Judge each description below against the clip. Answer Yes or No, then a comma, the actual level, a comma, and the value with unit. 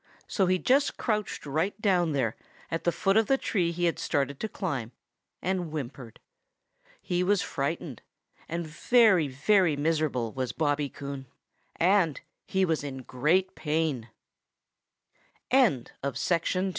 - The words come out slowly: Yes, slow, 130 wpm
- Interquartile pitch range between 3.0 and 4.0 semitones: No, average, 5.0 semitones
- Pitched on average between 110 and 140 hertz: No, medium, 165 Hz